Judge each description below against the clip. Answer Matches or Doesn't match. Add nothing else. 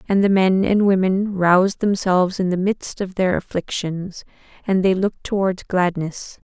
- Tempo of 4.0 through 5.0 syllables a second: Matches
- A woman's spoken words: Matches